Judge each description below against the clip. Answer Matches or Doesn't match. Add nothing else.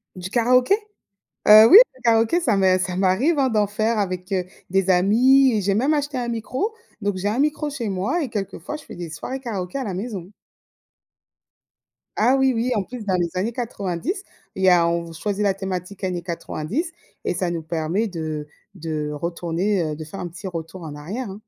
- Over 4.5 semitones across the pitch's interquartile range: Matches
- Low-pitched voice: Doesn't match